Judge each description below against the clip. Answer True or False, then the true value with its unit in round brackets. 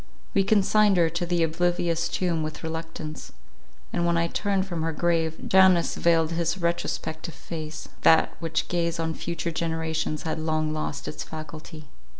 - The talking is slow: False (155 wpm)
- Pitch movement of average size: False (1.4 semitones)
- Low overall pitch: False (165 Hz)